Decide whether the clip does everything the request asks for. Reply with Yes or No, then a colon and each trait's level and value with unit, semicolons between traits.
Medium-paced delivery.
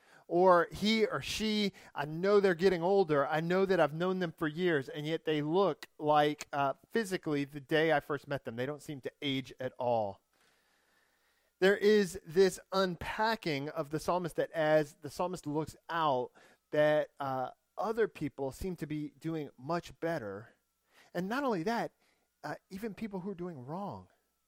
Yes: average, 175 wpm